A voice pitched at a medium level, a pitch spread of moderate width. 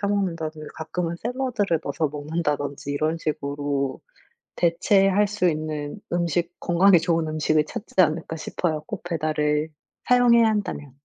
Yes: medium, 165 Hz; average, 3.9 semitones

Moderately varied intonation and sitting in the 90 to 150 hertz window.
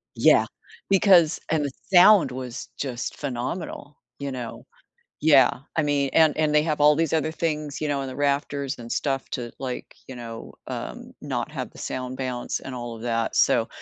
Yes: average, 3.3 semitones; medium, 140 Hz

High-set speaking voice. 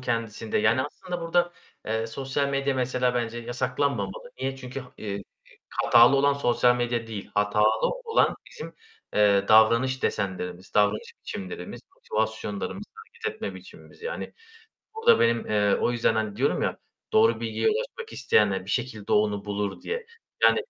No: low, 120 Hz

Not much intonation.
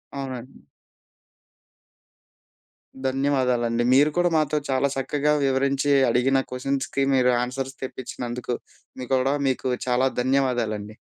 Yes: narrow, 1.6 semitones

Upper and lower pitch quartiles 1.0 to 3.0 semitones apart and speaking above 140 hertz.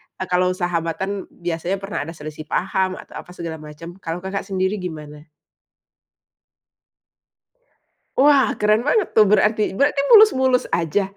No: average, 4.0 semitones; medium, 185 Hz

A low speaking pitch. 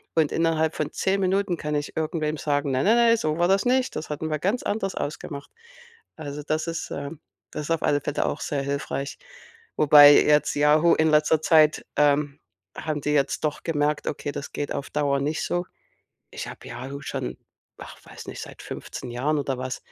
No: medium, 150 Hz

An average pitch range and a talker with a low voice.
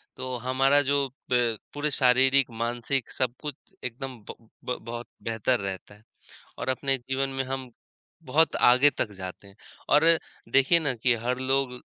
No: narrow, 2.3 semitones; low, 130 Hz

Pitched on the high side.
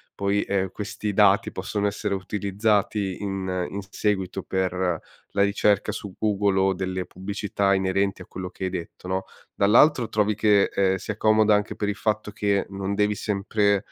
No: low, 100 Hz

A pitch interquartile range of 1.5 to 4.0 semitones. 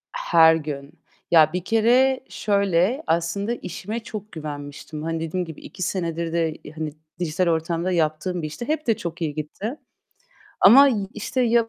No: wide, 5.4 semitones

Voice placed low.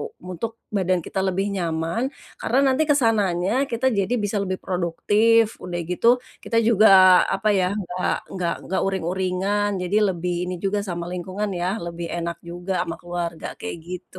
No: medium, 185 Hz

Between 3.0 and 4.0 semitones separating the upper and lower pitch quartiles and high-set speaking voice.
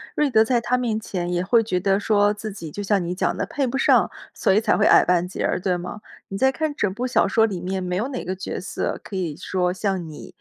Yes: average, 3.7 semitones; high, 200 Hz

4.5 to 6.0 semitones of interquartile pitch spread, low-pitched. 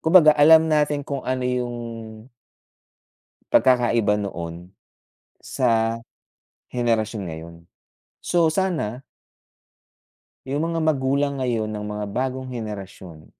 Yes: wide, 5.4 semitones; low, 125 Hz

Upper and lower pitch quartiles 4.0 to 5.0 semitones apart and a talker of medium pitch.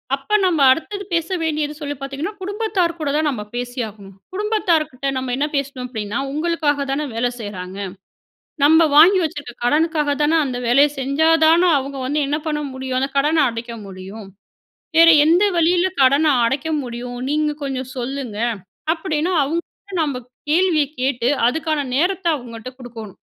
No: average, 4.4 semitones; very high, 285 Hz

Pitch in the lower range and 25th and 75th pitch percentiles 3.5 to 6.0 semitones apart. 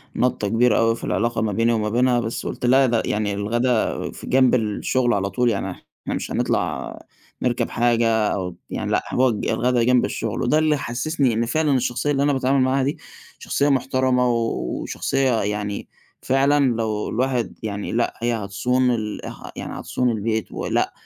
No: low, 120 Hz; average, 2.7 semitones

